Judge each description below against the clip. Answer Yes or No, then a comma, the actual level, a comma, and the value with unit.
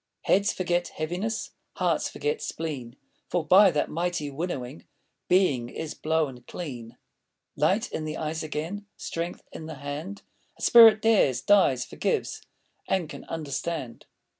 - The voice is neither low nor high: Yes, medium, 160 Hz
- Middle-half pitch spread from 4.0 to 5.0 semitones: Yes, average, 4.3 semitones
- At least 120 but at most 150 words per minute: Yes, slow, 135 wpm